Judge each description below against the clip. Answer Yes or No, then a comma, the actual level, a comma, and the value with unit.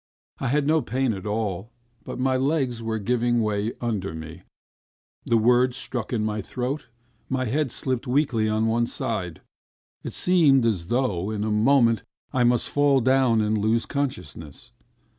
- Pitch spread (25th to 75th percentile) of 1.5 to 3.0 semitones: No, average, 3.5 semitones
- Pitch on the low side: Yes, low, 120 Hz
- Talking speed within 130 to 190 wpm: Yes, average, 160 wpm